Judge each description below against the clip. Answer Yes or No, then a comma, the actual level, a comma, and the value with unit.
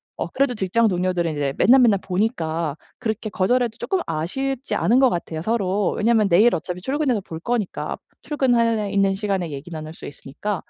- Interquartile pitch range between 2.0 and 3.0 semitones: No, wide, 5.5 semitones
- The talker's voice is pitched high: Yes, high, 200 Hz